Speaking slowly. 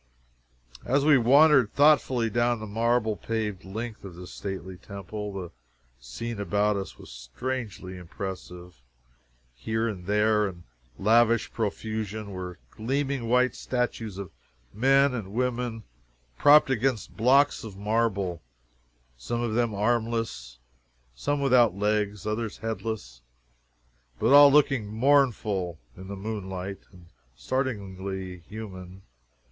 Yes: slow, 120 wpm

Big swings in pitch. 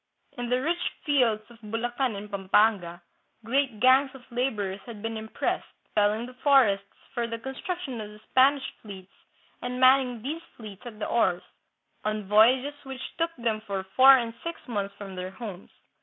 No: average, 4.0 semitones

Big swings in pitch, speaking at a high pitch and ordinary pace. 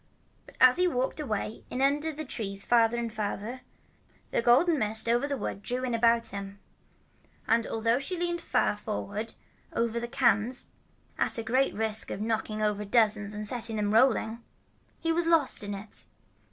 No: average, 3.3 semitones; high, 230 Hz; average, 180 wpm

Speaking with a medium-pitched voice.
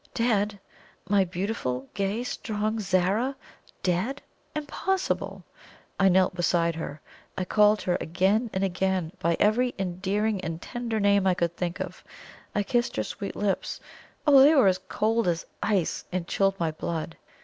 No: high, 195 Hz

